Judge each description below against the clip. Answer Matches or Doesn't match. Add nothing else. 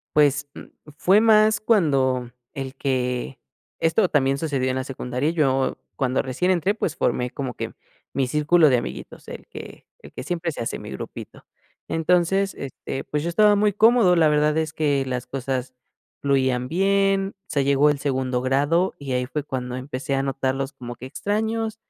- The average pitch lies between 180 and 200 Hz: Doesn't match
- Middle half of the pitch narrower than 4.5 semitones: Doesn't match